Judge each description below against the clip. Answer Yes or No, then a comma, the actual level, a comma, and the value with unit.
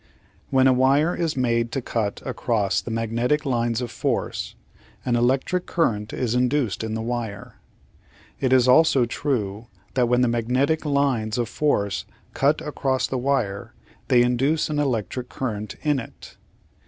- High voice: No, low, 125 Hz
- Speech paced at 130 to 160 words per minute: Yes, average, 150 wpm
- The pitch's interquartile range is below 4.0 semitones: Yes, average, 3.2 semitones